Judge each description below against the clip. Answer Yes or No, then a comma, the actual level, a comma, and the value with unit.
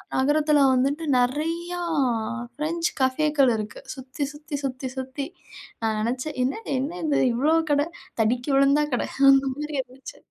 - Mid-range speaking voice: No, very high, 275 Hz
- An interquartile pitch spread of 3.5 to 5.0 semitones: No, average, 2.8 semitones